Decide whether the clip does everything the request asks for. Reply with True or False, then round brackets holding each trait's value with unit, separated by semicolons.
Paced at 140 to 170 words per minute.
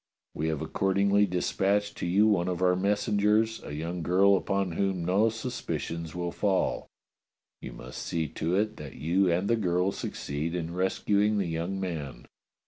True (165 wpm)